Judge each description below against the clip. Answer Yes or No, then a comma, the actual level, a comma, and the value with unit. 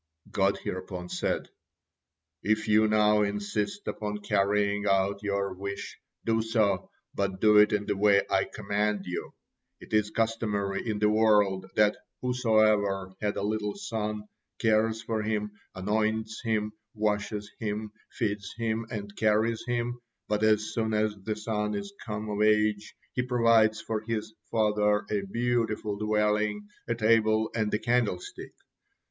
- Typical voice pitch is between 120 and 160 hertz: No, low, 105 Hz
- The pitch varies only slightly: Yes, narrow, 1.2 semitones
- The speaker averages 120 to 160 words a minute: Yes, average, 145 wpm